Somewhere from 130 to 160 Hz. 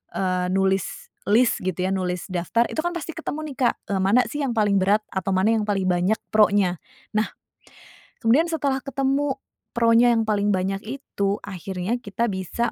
No: high, 210 Hz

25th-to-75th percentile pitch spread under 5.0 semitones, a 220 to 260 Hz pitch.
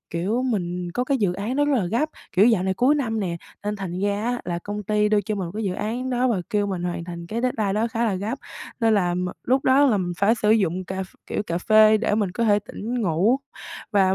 No: average, 3.9 semitones; high, 210 Hz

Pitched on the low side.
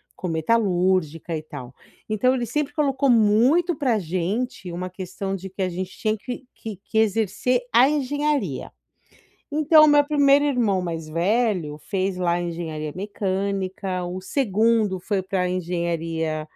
No: high, 195 Hz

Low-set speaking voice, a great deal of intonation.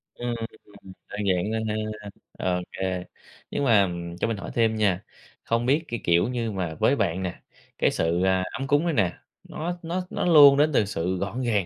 Yes: low, 110 Hz; wide, 6.0 semitones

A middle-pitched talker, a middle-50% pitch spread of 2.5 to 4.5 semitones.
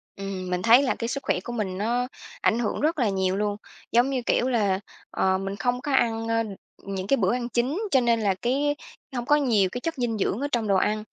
No: high, 230 Hz; average, 4.0 semitones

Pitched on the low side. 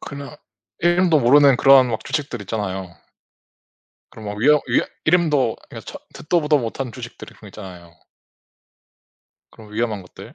Yes: low, 125 Hz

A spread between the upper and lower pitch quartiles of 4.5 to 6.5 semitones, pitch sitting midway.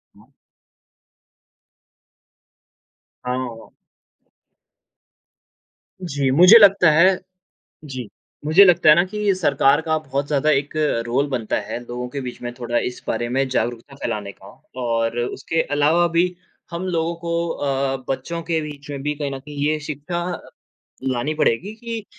Yes: average, 4.9 semitones; medium, 145 Hz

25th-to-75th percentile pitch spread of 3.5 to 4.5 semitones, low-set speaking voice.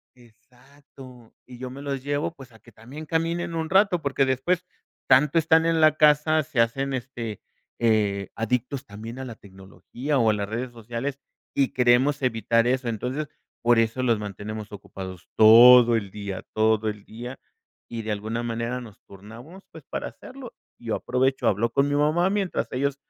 Yes: average, 4.1 semitones; low, 125 Hz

